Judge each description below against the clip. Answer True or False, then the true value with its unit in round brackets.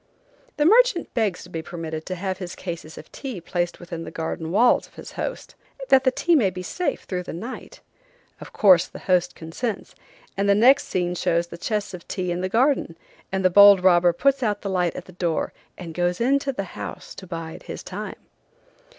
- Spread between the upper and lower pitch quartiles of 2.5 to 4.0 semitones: False (4.8 semitones)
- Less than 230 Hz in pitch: True (185 Hz)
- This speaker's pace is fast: True (210 wpm)